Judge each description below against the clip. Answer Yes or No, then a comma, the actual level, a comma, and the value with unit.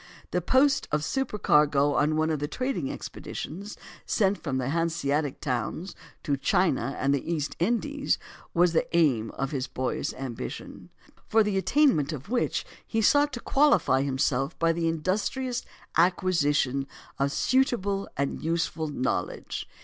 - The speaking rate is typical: Yes, average, 145 wpm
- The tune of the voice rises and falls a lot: Yes, wide, 6.5 semitones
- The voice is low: No, medium, 165 Hz